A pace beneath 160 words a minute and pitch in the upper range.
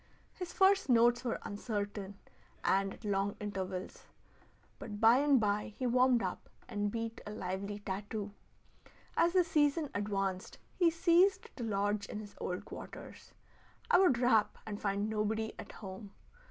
Yes: average, 150 wpm; high, 215 Hz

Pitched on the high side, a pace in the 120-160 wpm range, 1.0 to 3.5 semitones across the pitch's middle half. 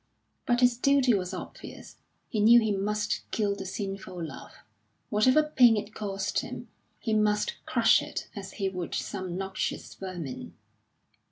Yes: high, 205 Hz; average, 150 wpm; average, 2.8 semitones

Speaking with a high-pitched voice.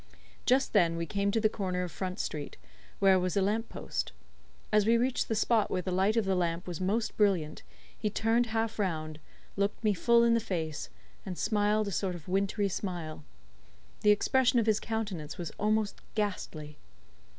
Yes: high, 200 Hz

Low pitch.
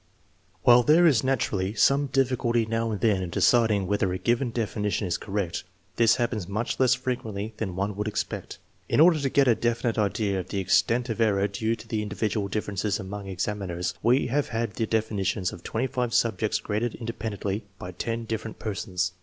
Yes: low, 110 Hz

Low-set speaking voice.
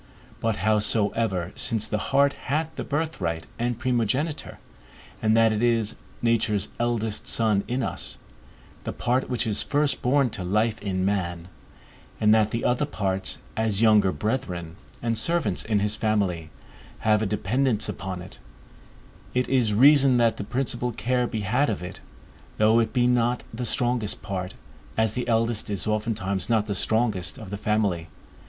Yes: low, 110 Hz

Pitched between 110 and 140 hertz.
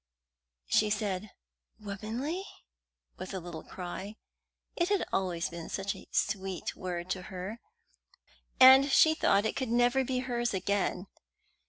No: high, 205 Hz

